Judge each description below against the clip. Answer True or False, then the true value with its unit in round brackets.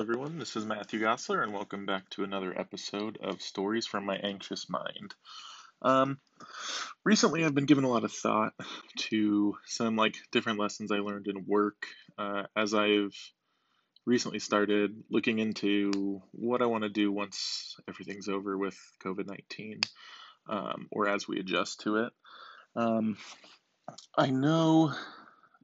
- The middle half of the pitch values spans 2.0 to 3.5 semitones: True (2.5 semitones)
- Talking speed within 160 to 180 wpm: False (145 wpm)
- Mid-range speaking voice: False (105 Hz)